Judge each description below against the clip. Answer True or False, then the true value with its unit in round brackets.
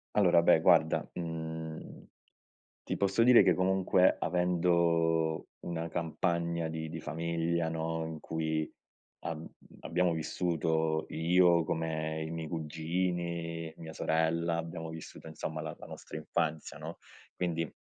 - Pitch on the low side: True (80 Hz)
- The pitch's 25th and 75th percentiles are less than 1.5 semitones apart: True (1.1 semitones)